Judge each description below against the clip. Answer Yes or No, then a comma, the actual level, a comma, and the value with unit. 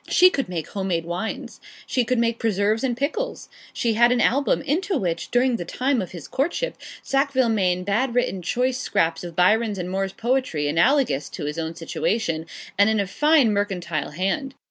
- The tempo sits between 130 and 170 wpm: No, average, 190 wpm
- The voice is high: Yes, high, 220 Hz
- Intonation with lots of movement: Yes, wide, 6.5 semitones